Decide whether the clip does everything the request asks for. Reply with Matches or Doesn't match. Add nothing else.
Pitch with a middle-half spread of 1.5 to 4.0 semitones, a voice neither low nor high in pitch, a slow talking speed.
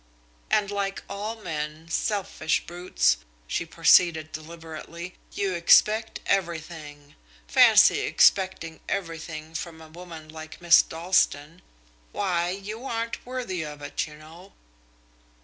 Matches